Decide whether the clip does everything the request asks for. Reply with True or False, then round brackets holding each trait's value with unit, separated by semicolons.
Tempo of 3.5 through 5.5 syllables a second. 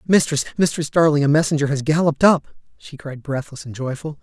False (5.9 syllables/s)